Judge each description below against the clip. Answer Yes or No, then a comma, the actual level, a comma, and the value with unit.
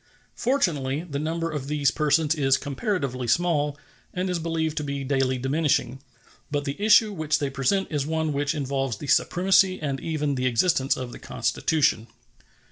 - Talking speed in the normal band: Yes, average, 165 wpm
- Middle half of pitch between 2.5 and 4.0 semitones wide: Yes, average, 3.3 semitones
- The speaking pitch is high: No, medium, 145 Hz